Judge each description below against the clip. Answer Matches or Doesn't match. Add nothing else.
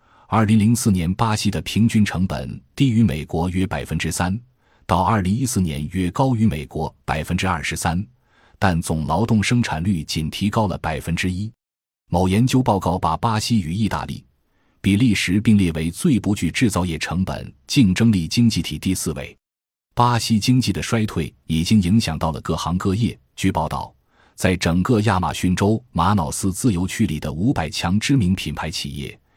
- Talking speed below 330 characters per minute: Matches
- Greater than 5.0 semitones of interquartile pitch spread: Matches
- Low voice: Matches